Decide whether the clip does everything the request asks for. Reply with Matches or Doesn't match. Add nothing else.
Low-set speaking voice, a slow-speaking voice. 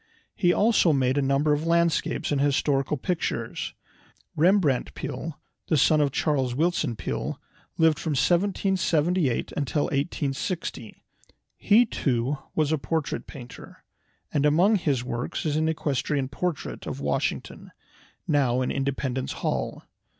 Doesn't match